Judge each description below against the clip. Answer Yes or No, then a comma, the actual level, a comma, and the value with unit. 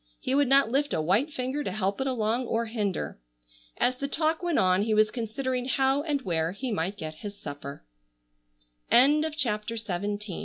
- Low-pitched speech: No, high, 240 Hz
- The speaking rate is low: No, average, 160 wpm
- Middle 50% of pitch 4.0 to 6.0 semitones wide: Yes, average, 5.2 semitones